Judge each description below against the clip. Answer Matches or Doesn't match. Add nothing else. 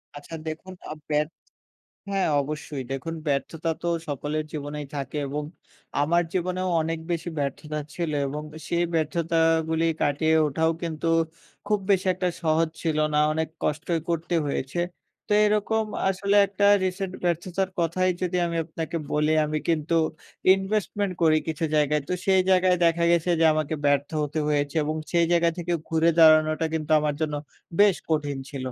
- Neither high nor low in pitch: Matches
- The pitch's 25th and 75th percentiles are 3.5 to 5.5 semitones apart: Doesn't match